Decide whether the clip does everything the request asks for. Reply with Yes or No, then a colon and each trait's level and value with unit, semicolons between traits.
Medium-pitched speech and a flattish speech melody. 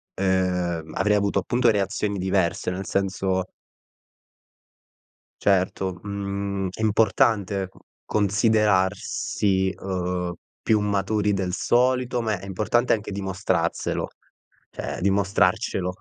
No: low, 100 Hz; narrow, 1.9 semitones